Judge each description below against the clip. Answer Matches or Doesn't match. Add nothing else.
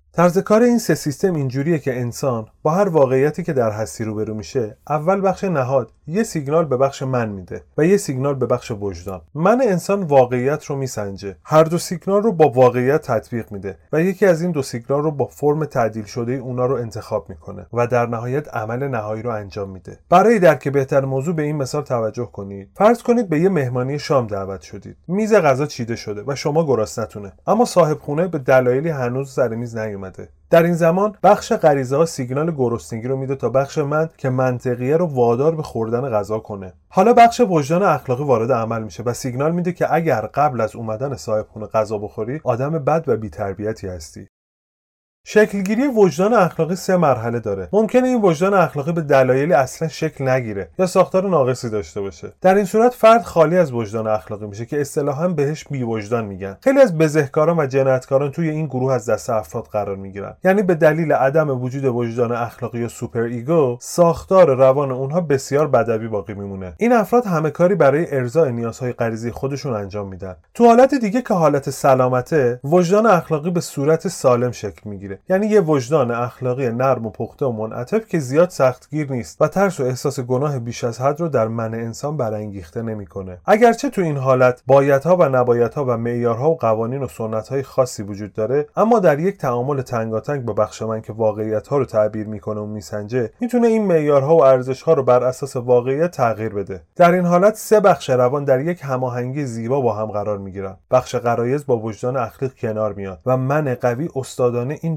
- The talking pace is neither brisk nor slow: Doesn't match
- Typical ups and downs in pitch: Doesn't match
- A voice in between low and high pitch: Doesn't match